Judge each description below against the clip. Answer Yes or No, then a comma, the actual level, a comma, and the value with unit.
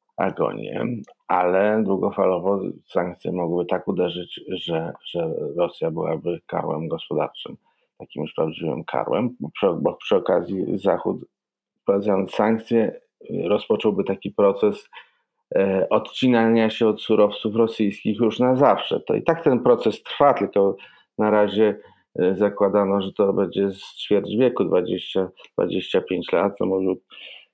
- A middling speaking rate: Yes, average, 120 wpm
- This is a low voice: Yes, low, 105 Hz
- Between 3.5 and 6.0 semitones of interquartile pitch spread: No, average, 3.1 semitones